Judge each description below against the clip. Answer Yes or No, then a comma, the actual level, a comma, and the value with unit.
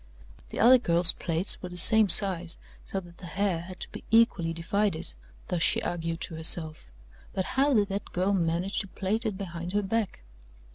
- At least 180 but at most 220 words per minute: Yes, average, 190 wpm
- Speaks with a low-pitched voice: No, medium, 185 Hz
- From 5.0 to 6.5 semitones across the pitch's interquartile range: No, average, 3.3 semitones